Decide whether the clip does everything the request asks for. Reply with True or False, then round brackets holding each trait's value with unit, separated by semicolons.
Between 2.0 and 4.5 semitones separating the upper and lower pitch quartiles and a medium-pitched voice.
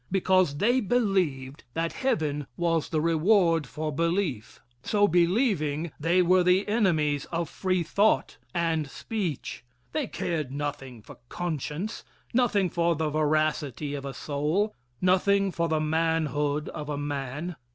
True (4.0 semitones; 165 Hz)